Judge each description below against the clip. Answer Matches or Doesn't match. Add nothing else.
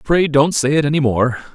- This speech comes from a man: Matches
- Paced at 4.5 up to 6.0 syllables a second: Matches